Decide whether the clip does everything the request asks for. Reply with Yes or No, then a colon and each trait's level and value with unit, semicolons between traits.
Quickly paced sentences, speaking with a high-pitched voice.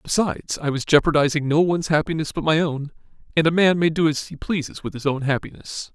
No: fast, 220 wpm; medium, 155 Hz